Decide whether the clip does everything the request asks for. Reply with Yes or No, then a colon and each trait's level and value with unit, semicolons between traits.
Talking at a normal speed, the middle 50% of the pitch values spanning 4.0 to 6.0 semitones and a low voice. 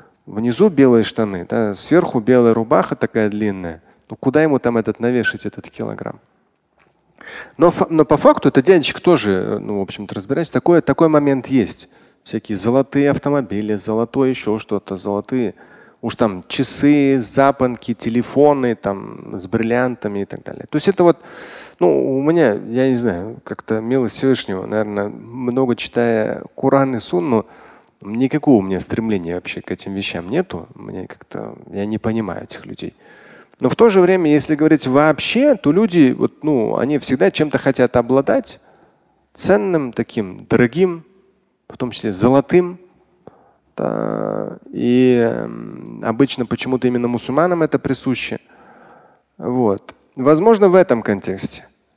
Yes: average, 140 wpm; average, 5.0 semitones; low, 125 Hz